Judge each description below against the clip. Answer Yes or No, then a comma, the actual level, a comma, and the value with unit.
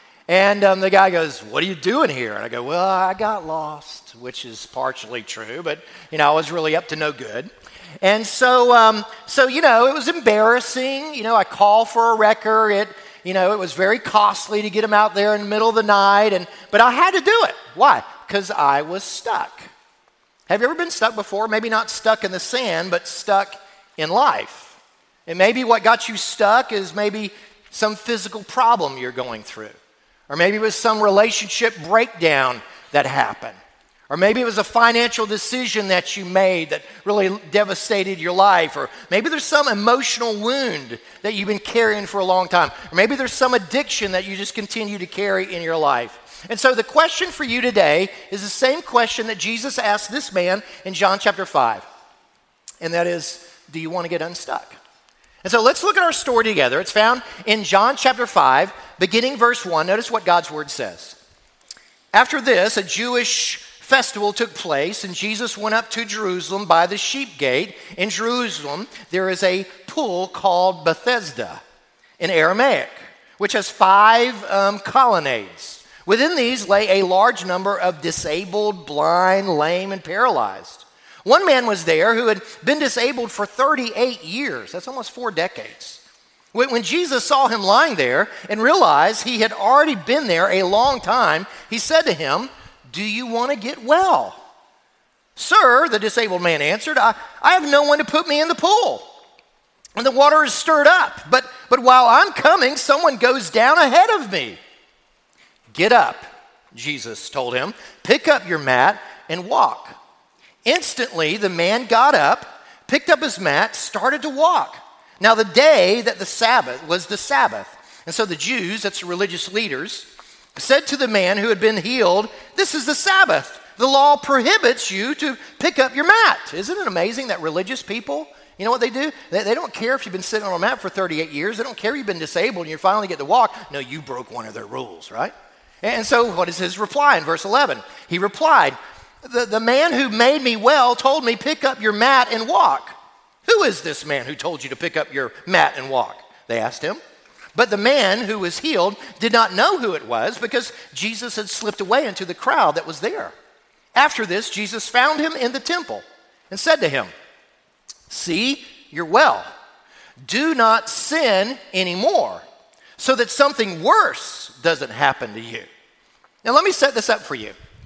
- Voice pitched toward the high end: Yes, high, 220 Hz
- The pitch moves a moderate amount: Yes, average, 5.0 semitones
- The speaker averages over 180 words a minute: Yes, average, 190 wpm